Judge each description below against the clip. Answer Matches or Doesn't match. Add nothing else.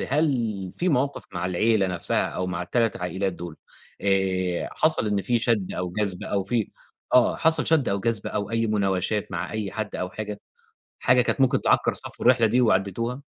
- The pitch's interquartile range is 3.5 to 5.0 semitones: Matches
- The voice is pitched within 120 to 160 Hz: Doesn't match